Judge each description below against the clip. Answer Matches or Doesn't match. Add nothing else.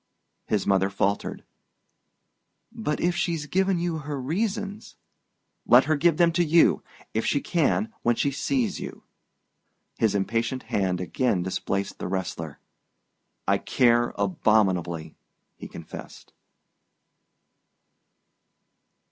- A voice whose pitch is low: Matches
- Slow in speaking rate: Matches